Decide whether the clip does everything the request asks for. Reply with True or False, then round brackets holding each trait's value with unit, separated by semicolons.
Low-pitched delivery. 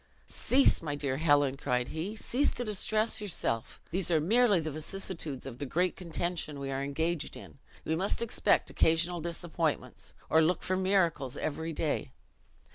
False (160 Hz)